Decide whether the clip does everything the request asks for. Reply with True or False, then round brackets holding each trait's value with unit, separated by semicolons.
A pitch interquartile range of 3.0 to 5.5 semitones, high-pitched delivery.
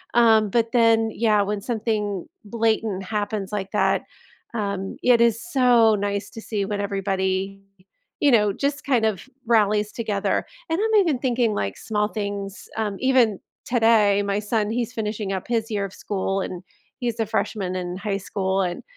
False (2.4 semitones; 210 Hz)